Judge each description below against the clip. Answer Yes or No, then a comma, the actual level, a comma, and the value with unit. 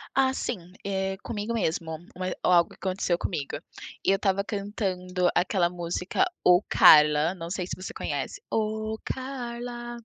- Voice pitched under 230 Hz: Yes, high, 190 Hz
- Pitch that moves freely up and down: No, average, 3.7 semitones